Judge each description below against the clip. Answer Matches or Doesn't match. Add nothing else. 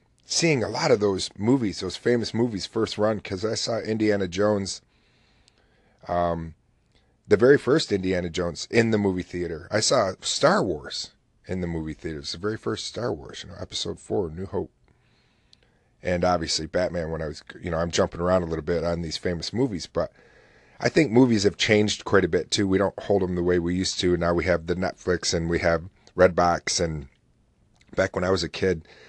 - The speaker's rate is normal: Doesn't match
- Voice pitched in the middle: Doesn't match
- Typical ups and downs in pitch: Matches